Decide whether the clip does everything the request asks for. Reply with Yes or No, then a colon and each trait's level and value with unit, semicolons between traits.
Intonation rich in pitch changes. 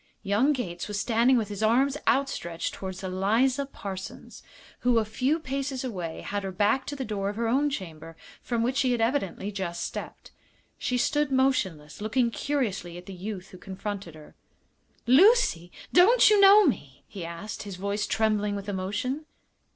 Yes: wide, 5.7 semitones